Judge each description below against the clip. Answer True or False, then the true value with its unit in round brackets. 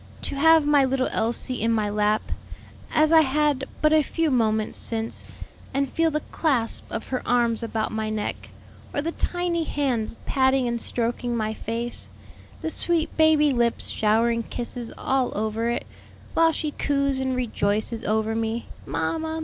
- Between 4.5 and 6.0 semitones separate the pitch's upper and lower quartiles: True (4.8 semitones)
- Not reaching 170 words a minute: True (160 wpm)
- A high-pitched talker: True (250 Hz)